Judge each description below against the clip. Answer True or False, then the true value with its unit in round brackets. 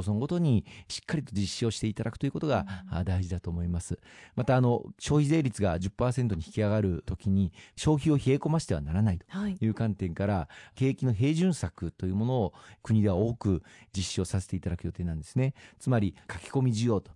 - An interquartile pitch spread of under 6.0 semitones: True (5.2 semitones)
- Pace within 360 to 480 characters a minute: True (405 characters per minute)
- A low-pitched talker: True (105 Hz)